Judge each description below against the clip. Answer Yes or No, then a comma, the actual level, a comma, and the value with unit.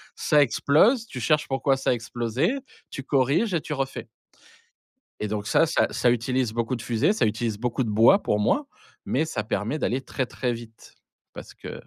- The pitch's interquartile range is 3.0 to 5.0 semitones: Yes, average, 4.3 semitones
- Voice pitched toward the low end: Yes, low, 125 Hz